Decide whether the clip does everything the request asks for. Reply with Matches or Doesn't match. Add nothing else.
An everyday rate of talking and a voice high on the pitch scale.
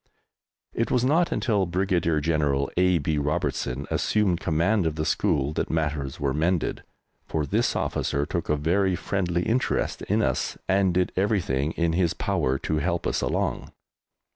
Doesn't match